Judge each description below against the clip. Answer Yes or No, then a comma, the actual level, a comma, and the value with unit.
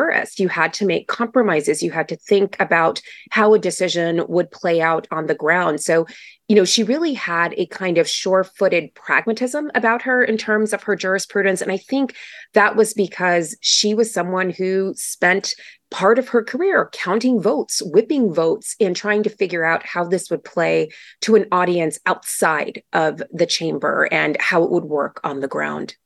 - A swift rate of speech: No, average, 185 wpm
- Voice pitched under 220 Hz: Yes, high, 190 Hz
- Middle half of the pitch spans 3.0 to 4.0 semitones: No, average, 4.4 semitones